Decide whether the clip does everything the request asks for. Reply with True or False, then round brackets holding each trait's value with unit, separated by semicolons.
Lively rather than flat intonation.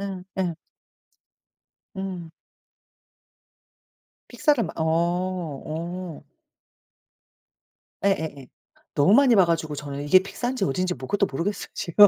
False (3.6 semitones)